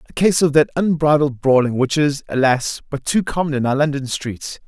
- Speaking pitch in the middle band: Yes, medium, 145 Hz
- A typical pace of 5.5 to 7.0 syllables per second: No, 5.2 syllables/s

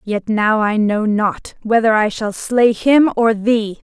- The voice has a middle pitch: No, high, 220 Hz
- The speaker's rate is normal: Yes, average, 185 wpm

